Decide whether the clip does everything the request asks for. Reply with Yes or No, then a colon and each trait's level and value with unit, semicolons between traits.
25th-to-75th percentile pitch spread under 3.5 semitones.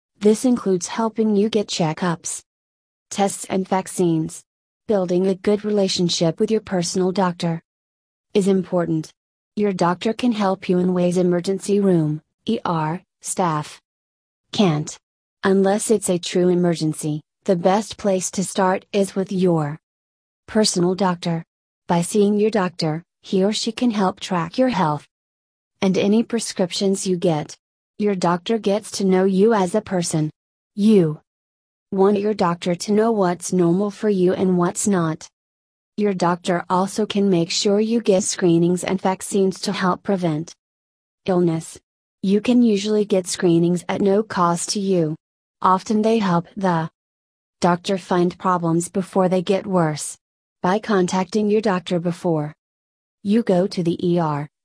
Yes: average, 3.0 semitones